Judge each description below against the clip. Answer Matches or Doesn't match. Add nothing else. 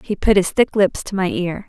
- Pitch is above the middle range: Matches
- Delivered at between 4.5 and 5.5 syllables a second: Matches